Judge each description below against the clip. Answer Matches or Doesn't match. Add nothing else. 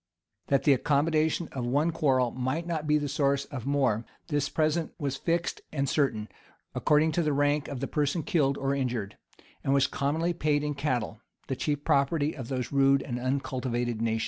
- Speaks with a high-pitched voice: Doesn't match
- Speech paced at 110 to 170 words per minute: Doesn't match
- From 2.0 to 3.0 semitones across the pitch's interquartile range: Matches